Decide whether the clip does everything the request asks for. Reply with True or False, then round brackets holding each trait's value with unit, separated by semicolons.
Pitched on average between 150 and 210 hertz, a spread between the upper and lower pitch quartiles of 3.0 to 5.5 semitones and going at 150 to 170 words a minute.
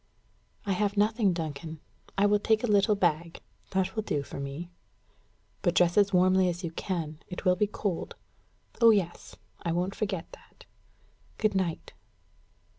True (185 Hz; 3.3 semitones; 160 wpm)